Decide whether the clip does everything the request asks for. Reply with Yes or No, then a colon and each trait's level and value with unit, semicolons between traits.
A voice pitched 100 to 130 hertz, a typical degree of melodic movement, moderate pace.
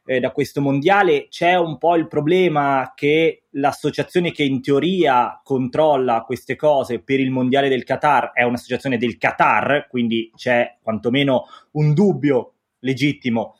No: medium, 140 Hz; average, 3.2 semitones; average, 135 wpm